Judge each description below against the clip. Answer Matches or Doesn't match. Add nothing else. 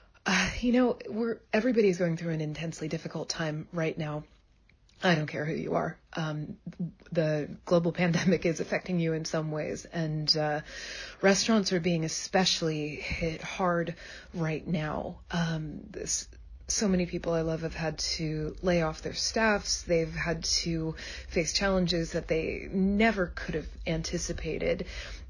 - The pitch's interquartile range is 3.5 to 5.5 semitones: Doesn't match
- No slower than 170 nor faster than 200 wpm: Doesn't match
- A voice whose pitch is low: Doesn't match